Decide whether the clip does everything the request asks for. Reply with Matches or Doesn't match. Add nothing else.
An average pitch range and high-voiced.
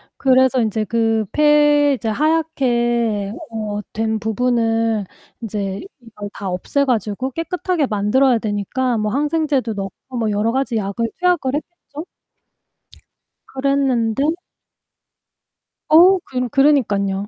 Matches